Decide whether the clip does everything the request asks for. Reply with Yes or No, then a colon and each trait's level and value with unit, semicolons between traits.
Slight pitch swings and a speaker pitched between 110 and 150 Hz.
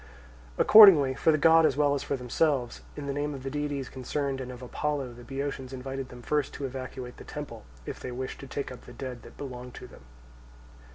Yes: narrow, 2.3 semitones; low, 135 Hz